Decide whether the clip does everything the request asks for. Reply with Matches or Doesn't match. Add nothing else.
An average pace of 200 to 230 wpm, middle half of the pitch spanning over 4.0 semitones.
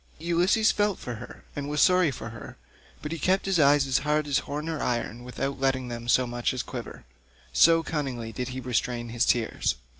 Matches